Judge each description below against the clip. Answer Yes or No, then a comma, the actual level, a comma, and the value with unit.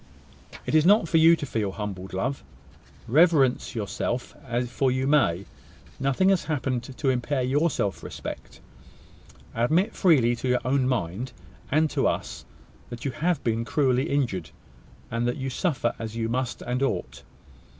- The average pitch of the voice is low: Yes, low, 130 Hz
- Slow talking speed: No, average, 155 wpm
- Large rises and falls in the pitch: No, average, 4.2 semitones